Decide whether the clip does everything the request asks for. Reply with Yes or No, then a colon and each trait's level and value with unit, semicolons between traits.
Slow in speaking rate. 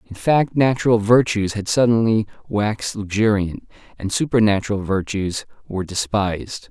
Yes: slow, 115 wpm